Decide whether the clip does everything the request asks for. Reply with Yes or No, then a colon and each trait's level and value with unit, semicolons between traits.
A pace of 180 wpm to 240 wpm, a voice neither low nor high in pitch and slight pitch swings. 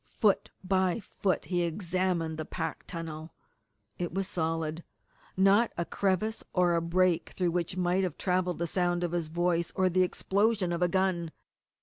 No: average, 165 wpm; medium, 180 Hz; narrow, 1.9 semitones